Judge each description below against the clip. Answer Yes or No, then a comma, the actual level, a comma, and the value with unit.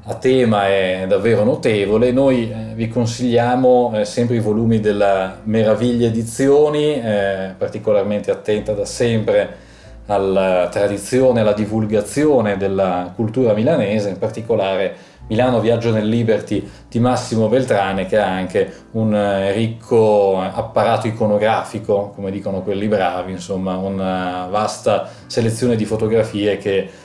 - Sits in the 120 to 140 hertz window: No, low, 110 Hz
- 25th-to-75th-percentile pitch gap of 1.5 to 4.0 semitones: Yes, average, 2.9 semitones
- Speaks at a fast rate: No, slow, 115 wpm